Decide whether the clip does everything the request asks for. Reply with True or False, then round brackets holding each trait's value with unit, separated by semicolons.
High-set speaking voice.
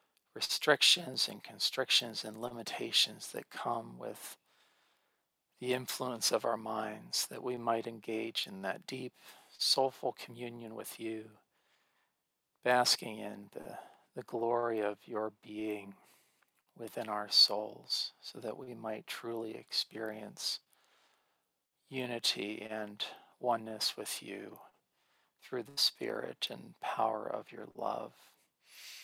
False (115 Hz)